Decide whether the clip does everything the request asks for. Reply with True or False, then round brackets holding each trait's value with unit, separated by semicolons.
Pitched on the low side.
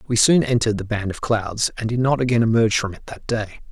True (115 Hz)